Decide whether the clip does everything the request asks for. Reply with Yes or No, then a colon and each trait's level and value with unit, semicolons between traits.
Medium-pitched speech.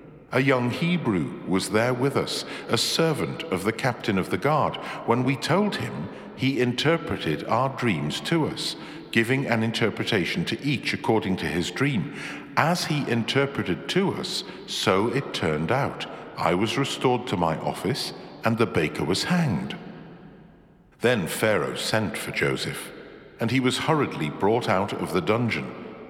No: low, 125 Hz